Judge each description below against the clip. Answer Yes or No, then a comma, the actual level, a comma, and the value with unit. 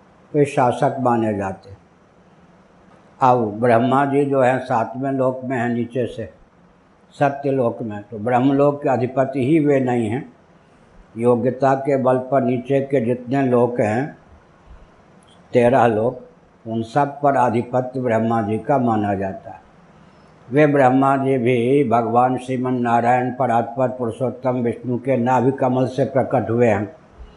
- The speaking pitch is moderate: No, low, 125 Hz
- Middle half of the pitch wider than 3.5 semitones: No, average, 2.7 semitones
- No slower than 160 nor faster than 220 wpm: No, average, 140 wpm